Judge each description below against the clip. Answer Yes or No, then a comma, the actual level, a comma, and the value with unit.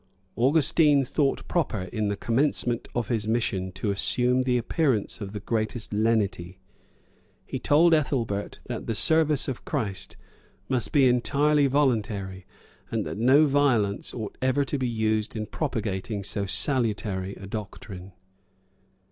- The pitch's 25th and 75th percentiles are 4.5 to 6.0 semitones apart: Yes, average, 4.9 semitones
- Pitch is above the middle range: No, low, 115 Hz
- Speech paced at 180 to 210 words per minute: No, average, 140 wpm